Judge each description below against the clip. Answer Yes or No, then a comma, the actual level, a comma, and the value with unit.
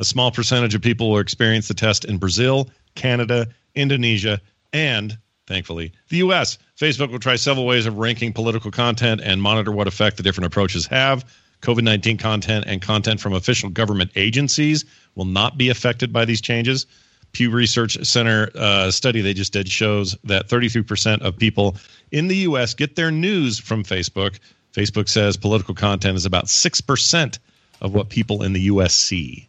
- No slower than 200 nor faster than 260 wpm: No, average, 175 wpm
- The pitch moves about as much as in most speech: Yes, average, 3.5 semitones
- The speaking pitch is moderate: No, low, 110 Hz